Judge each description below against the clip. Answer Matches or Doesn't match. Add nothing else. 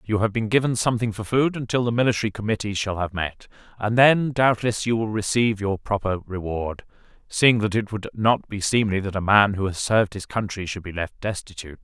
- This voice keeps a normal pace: Doesn't match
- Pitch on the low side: Matches